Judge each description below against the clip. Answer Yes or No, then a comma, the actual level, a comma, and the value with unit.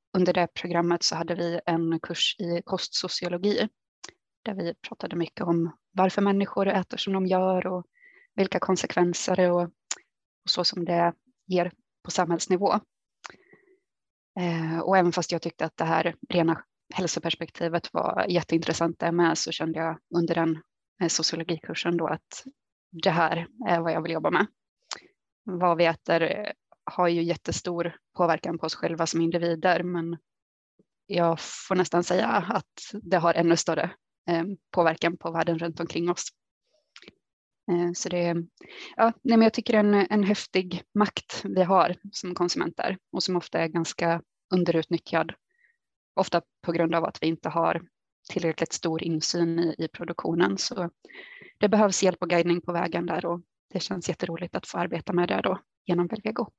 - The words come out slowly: No, average, 155 wpm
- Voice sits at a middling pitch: Yes, medium, 175 Hz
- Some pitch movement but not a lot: No, narrow, 2.0 semitones